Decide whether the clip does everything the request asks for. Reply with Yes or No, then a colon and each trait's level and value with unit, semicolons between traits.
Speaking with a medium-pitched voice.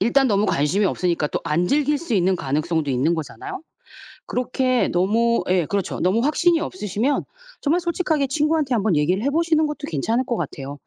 No: high, 230 Hz